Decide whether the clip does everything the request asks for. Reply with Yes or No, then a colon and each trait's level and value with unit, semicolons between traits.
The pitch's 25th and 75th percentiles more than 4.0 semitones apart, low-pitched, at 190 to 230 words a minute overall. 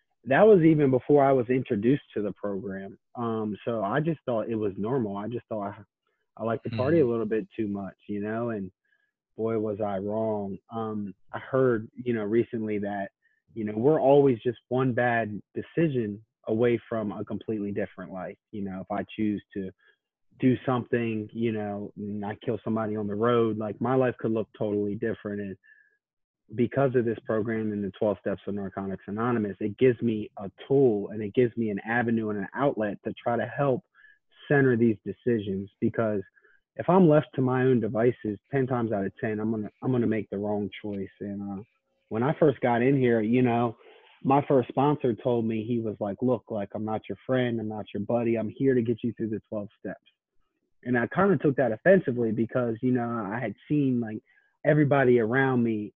No: average, 3.3 semitones; low, 115 Hz; fast, 205 wpm